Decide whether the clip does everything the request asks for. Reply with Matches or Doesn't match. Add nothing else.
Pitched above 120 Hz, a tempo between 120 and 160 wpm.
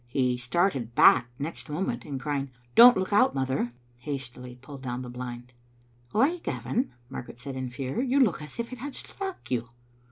Doesn't match